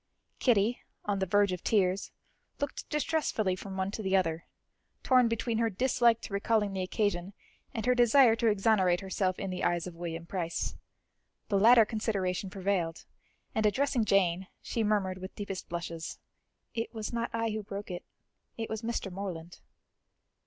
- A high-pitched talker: Yes, high, 200 Hz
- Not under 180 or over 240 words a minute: No, average, 165 wpm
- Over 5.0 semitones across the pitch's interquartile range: No, average, 3.5 semitones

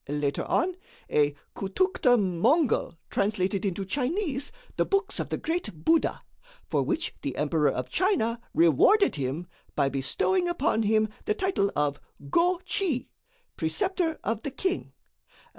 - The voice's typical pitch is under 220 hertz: No, high, 230 Hz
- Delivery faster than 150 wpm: No, slow, 135 wpm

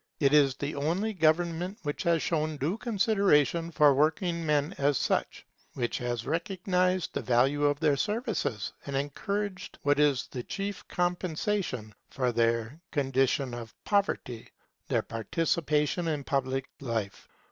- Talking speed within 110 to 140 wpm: Yes, slow, 135 wpm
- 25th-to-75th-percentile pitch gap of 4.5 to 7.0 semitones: Yes, average, 4.9 semitones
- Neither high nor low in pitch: Yes, medium, 150 Hz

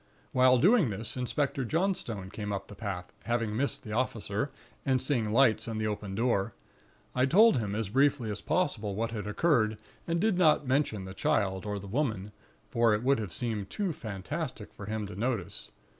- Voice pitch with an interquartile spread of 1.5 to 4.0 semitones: No, average, 4.8 semitones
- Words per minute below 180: No, average, 190 wpm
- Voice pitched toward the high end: No, low, 115 Hz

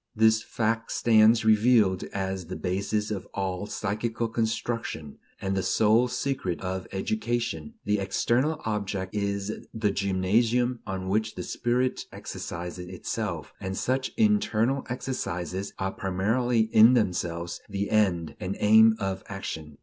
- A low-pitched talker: Yes, low, 105 Hz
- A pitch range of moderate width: Yes, average, 3.5 semitones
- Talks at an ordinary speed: No, slow, 130 wpm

